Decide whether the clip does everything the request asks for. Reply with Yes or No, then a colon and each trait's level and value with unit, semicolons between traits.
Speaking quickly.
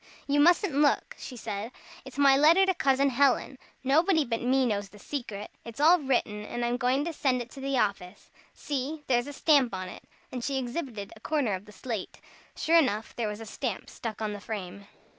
Yes: fast, 210 wpm